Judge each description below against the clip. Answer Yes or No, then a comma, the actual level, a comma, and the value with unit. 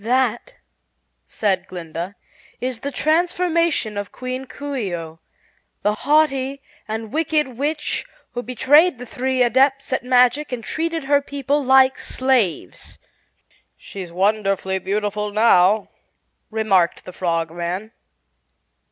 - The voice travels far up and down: Yes, wide, 5.8 semitones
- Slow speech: Yes, slow, 115 wpm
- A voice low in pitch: No, high, 245 Hz